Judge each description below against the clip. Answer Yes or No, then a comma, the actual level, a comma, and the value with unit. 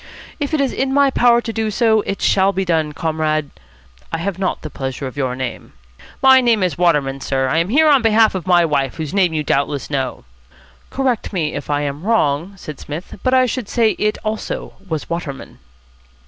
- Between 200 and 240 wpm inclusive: Yes, fast, 205 wpm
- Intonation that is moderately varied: No, wide, 7.3 semitones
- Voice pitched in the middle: Yes, medium, 175 Hz